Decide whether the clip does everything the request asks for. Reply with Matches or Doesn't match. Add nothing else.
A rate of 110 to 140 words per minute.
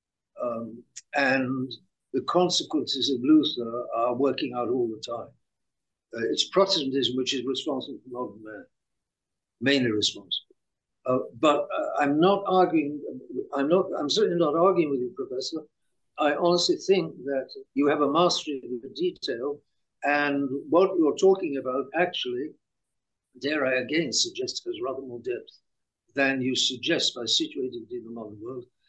Doesn't match